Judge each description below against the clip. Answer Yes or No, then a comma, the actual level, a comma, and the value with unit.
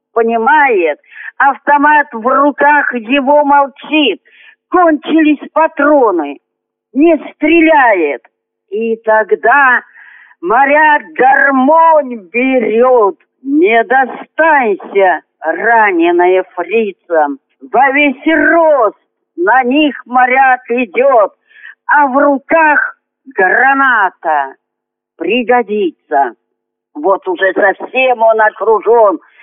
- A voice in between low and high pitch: No, very high, 275 Hz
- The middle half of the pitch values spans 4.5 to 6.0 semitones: Yes, average, 5.3 semitones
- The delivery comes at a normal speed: No, slow, 75 wpm